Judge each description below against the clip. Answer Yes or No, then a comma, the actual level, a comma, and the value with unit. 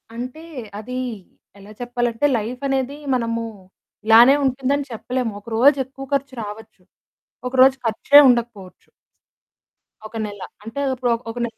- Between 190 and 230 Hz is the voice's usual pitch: No, high, 245 Hz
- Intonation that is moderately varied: Yes, average, 3.0 semitones